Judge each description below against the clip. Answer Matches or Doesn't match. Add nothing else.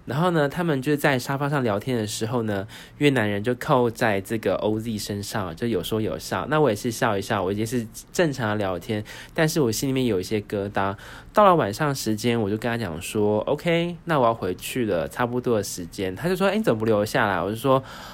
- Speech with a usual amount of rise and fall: Matches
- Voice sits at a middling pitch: Doesn't match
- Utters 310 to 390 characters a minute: Matches